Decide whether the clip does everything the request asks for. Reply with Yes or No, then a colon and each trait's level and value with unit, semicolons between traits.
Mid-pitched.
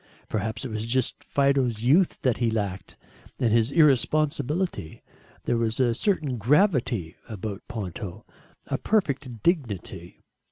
No: low, 120 Hz